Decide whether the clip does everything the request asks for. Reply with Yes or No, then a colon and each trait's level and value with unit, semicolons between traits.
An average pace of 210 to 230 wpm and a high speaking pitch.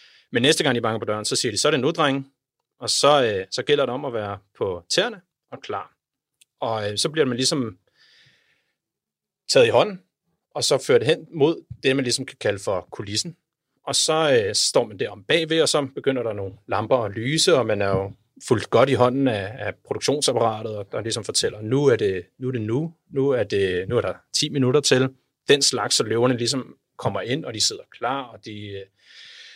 No: average, 220 wpm; low, 135 Hz